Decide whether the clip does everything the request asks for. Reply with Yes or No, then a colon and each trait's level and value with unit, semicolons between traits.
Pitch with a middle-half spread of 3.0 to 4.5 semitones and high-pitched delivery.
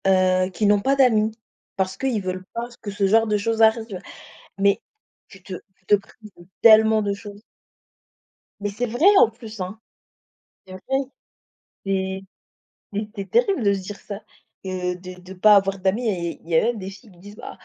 No: narrow, 2.6 semitones; high, 200 Hz